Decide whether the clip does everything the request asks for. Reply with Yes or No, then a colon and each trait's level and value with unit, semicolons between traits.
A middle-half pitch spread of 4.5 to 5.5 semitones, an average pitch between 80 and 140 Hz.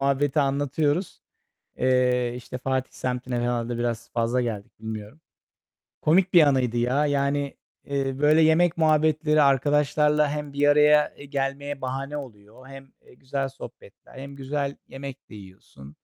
No: average, 2.9 semitones; low, 135 Hz